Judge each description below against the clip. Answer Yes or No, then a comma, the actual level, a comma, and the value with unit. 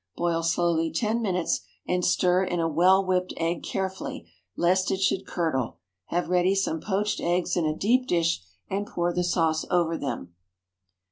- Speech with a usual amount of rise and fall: No, narrow, 2.3 semitones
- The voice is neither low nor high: Yes, medium, 175 Hz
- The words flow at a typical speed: Yes, average, 165 wpm